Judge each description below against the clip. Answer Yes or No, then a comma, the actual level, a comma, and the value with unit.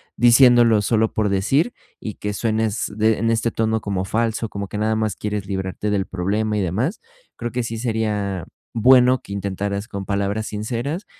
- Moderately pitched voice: No, low, 110 Hz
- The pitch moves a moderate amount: No, narrow, 2.3 semitones